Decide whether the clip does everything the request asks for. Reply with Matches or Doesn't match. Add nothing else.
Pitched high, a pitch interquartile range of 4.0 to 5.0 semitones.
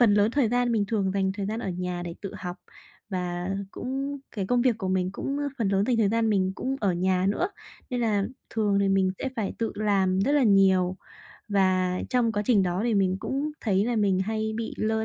Doesn't match